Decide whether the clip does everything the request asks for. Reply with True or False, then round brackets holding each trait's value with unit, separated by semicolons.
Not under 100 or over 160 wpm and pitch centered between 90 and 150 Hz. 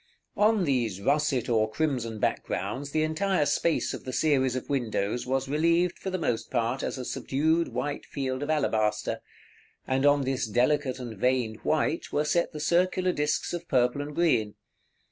False (180 wpm; 140 Hz)